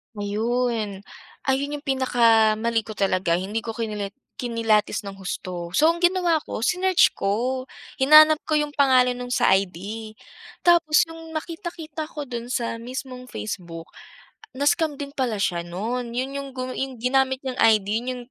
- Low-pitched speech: No, very high, 250 Hz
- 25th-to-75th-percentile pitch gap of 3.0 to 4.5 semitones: No, average, 4.9 semitones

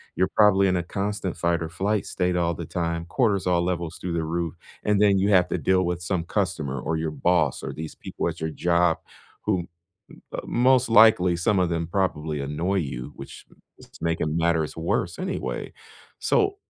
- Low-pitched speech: Yes, very low, 85 Hz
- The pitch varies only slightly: No, average, 3.0 semitones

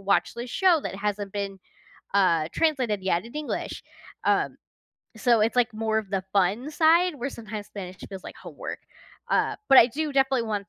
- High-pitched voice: Yes, high, 220 Hz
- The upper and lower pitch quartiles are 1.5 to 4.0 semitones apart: No, average, 5.1 semitones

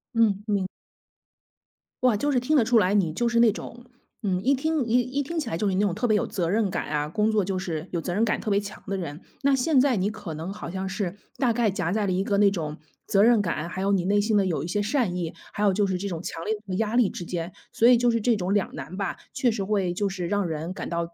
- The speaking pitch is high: Yes, high, 200 Hz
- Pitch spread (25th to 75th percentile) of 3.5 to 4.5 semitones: Yes, average, 4.0 semitones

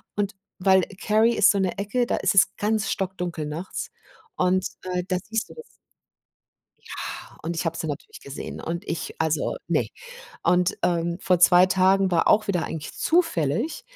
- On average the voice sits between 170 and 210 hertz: Yes, medium, 185 Hz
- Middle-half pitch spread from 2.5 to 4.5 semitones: Yes, average, 2.9 semitones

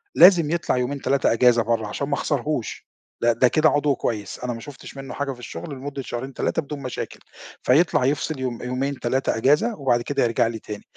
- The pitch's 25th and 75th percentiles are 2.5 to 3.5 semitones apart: Yes, average, 3.1 semitones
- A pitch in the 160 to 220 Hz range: No, low, 130 Hz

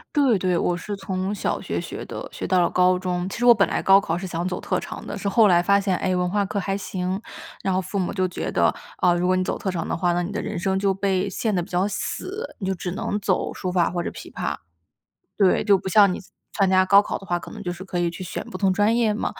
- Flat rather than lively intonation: Yes, narrow, 1.8 semitones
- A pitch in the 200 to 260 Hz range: No, high, 190 Hz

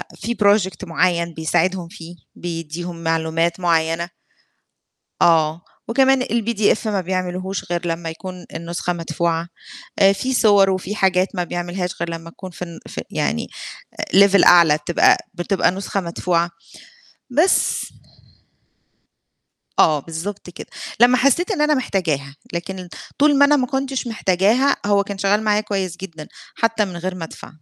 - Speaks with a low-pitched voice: No, medium, 185 Hz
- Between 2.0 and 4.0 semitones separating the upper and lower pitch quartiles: Yes, average, 3.4 semitones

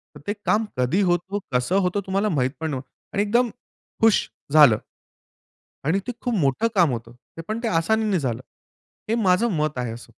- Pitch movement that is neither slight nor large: No, wide, 7.6 semitones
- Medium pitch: Yes, medium, 175 Hz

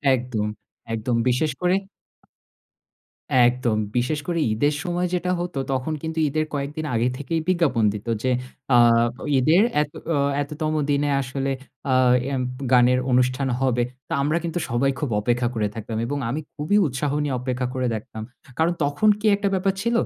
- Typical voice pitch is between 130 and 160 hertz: Yes, medium, 140 Hz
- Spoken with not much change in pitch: No, average, 4.3 semitones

